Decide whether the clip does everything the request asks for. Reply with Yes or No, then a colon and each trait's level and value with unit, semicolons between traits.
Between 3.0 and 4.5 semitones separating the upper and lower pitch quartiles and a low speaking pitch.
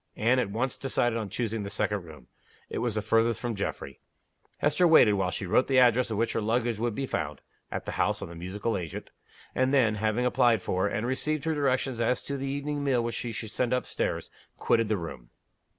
Yes: average, 3.7 semitones; low, 115 Hz